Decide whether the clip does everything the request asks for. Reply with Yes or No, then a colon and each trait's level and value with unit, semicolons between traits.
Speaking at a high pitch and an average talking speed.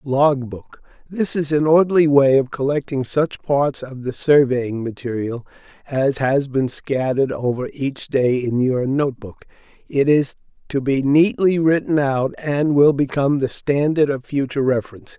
No: medium, 140 Hz; average, 160 wpm